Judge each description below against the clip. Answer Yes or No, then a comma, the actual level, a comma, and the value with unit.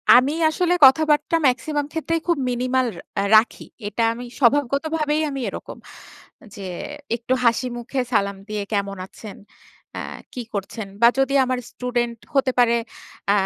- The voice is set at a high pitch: Yes, very high, 250 Hz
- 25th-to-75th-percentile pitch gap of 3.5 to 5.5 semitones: Yes, average, 3.9 semitones